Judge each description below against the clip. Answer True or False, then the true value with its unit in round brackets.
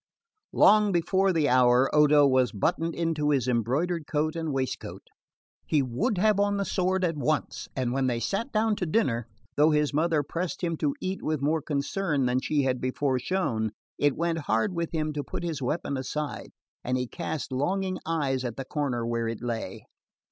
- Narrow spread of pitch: False (4.9 semitones)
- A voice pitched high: False (150 Hz)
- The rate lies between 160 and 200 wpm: True (190 wpm)